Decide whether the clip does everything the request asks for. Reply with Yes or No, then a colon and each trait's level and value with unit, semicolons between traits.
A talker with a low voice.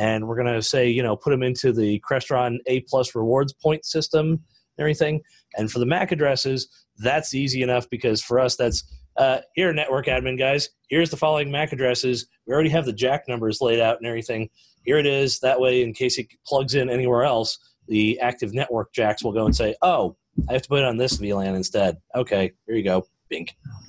Yes: low, 130 Hz